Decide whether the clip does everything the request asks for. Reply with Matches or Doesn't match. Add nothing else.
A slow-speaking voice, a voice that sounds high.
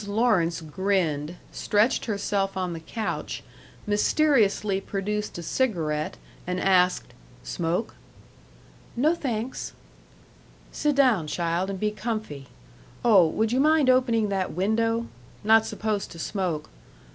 Matches